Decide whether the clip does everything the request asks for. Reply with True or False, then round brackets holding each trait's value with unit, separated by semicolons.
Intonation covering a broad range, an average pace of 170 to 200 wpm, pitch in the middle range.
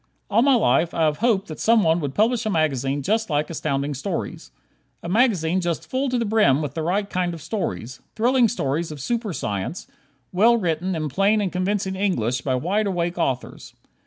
True (6.3 semitones; 190 wpm; 175 Hz)